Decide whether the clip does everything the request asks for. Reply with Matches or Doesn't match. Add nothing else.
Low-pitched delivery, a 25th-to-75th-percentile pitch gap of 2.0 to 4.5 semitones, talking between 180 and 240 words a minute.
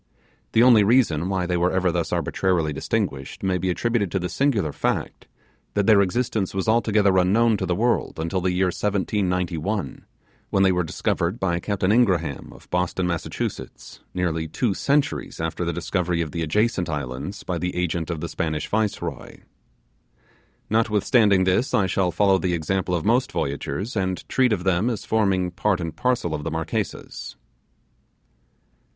Doesn't match